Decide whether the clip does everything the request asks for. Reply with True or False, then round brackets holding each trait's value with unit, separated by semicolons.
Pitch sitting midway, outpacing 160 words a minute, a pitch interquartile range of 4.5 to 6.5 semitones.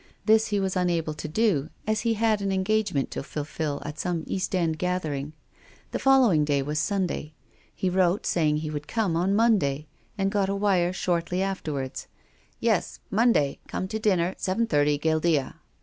True (180 Hz; 180 wpm; 4.8 semitones)